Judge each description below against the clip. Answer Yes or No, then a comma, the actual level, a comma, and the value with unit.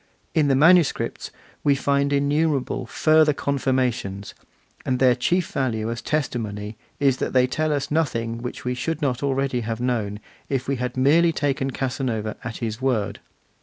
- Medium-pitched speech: No, low, 130 Hz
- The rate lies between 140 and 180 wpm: Yes, average, 160 wpm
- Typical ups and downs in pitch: Yes, average, 3.0 semitones